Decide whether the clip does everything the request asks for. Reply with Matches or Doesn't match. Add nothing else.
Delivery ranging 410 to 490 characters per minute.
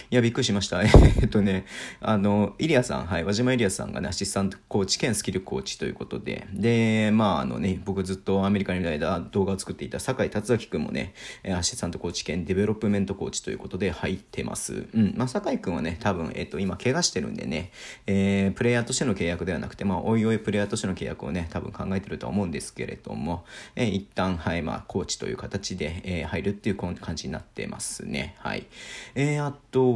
Matches